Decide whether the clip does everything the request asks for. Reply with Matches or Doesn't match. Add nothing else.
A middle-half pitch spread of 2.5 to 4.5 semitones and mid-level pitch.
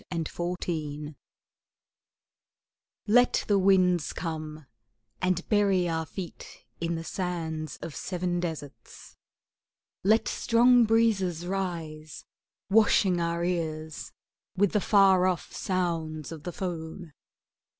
Matches